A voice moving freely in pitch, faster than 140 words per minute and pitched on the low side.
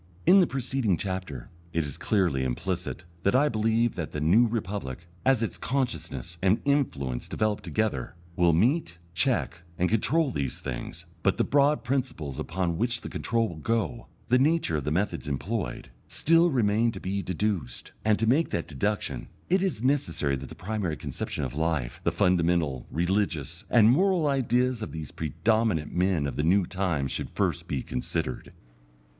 Yes: wide, 7.1 semitones; average, 170 wpm; low, 100 Hz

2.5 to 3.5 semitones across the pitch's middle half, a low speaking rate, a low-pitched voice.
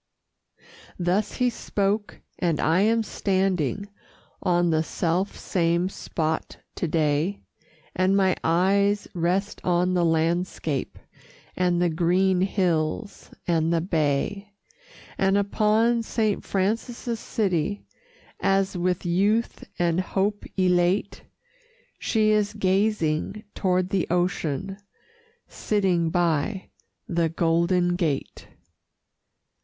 No: average, 2.9 semitones; slow, 100 wpm; medium, 185 Hz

